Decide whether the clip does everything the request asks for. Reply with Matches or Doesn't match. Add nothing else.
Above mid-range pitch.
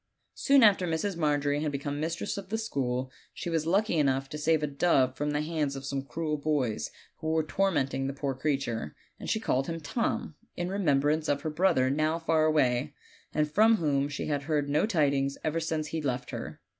Doesn't match